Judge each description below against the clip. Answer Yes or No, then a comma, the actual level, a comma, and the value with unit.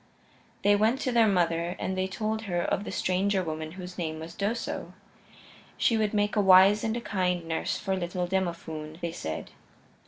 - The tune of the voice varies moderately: Yes, average, 3.3 semitones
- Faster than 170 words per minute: Yes, average, 185 wpm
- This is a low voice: No, medium, 185 Hz